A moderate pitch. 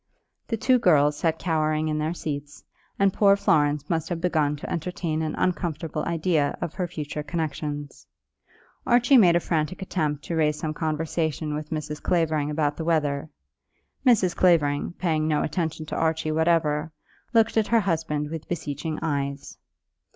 Yes: medium, 160 Hz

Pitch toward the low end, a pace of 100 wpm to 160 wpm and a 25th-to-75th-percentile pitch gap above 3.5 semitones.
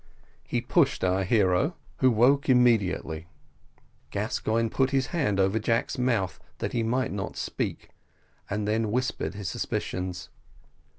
Yes: low, 110 Hz; slow, 135 wpm; average, 4.7 semitones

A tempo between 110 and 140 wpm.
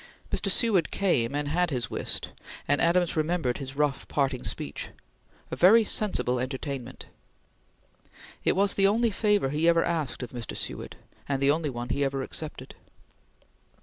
No: average, 155 wpm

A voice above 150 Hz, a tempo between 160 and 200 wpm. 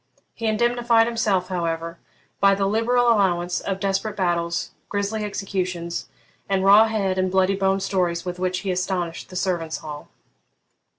No: high, 190 Hz; average, 145 wpm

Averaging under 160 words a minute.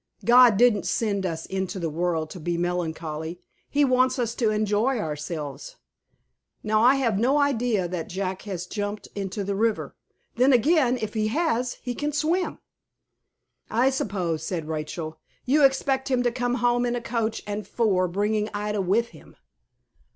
No: average, 165 wpm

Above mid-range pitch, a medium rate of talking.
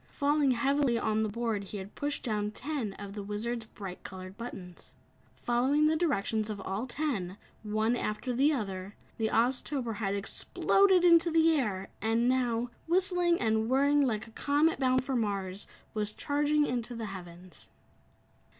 Yes: high, 235 Hz; average, 160 wpm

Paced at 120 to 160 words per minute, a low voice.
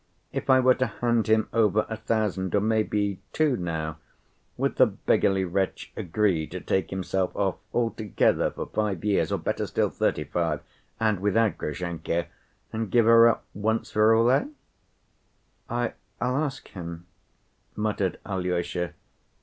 Yes: average, 140 wpm; low, 105 Hz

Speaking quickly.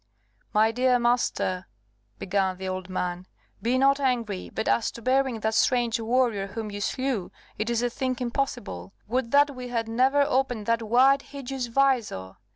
No: average, 165 wpm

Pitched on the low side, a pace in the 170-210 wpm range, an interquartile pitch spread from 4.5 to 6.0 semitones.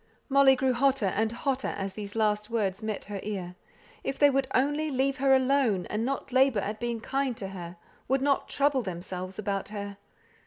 No: high, 230 Hz; average, 190 wpm; average, 5.0 semitones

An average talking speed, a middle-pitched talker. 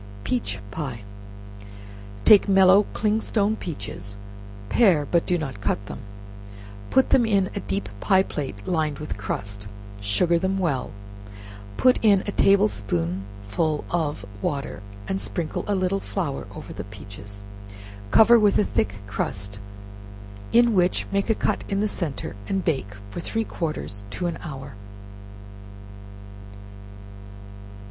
No: slow, 130 wpm; medium, 155 Hz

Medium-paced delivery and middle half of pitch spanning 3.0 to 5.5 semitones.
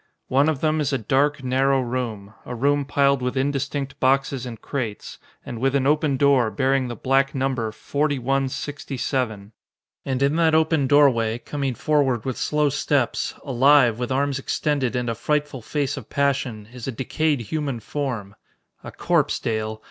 No: average, 165 wpm; narrow, 2.6 semitones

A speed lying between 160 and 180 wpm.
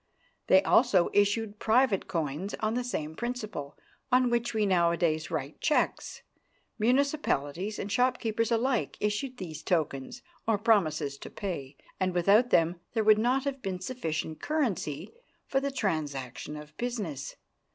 No: average, 140 wpm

